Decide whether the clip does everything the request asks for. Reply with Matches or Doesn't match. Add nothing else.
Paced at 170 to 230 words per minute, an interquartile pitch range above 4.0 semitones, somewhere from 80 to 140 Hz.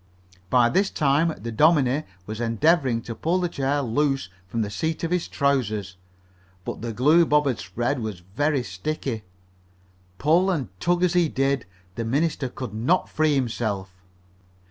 Doesn't match